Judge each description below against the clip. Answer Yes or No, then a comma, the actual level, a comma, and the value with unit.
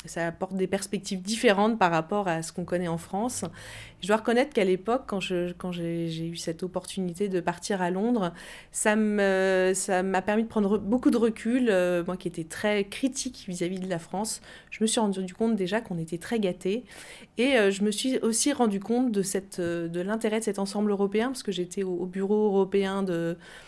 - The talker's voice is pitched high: Yes, high, 195 Hz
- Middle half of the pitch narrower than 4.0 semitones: Yes, average, 3.4 semitones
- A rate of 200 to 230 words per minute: Yes, average, 210 wpm